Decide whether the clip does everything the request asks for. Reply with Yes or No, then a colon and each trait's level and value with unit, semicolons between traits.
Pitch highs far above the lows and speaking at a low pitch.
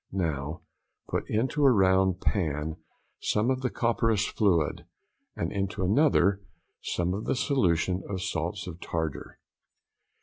No: average, 4.2 semitones; very low, 95 Hz